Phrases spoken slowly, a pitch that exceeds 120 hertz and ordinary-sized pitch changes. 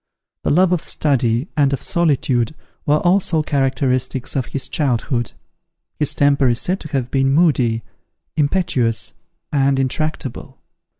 Yes: slow, 130 wpm; medium, 140 Hz; average, 3.3 semitones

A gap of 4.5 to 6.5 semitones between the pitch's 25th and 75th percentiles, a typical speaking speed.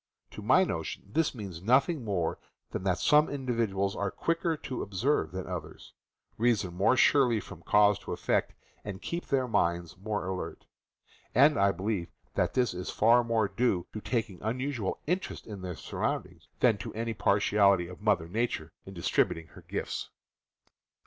Yes: average, 4.8 semitones; average, 170 wpm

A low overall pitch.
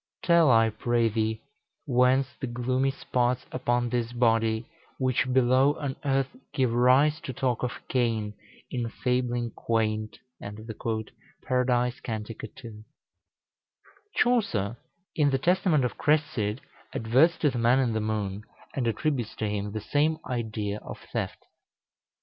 Yes: low, 120 Hz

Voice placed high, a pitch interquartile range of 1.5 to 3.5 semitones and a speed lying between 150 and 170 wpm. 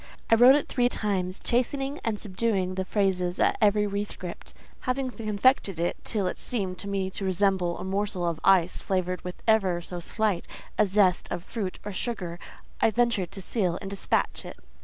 No: high, 195 Hz; average, 3.1 semitones; average, 185 wpm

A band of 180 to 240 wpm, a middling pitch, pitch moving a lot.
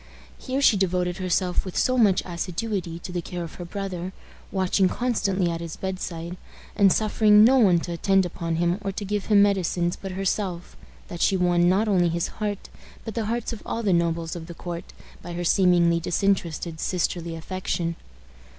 No: average, 185 wpm; medium, 180 Hz; average, 2.7 semitones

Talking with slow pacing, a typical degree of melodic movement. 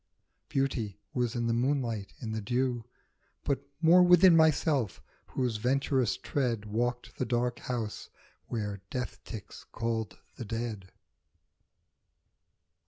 Yes: slow, 115 wpm; average, 3.1 semitones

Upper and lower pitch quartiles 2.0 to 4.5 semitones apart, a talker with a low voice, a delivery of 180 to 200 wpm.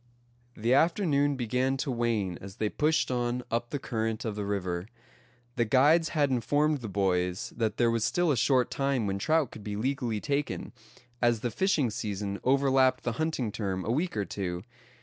No: average, 4.9 semitones; low, 120 Hz; average, 185 wpm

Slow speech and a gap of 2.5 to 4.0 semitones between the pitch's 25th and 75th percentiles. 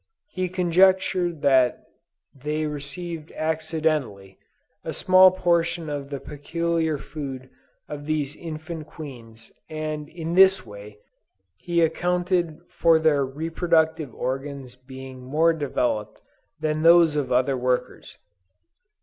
Yes: slow, 110 wpm; average, 3.7 semitones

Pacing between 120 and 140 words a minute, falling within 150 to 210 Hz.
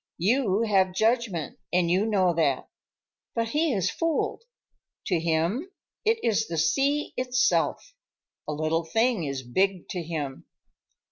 Yes: slow, 135 wpm; high, 190 Hz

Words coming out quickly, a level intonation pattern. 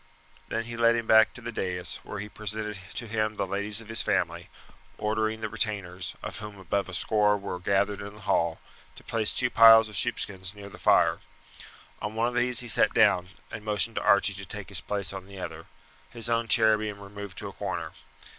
Yes: fast, 215 wpm; narrow, 2.1 semitones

